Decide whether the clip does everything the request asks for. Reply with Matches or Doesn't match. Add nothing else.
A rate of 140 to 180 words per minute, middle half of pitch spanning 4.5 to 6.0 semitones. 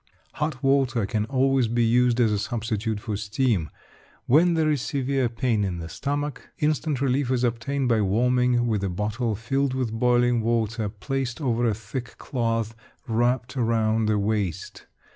Doesn't match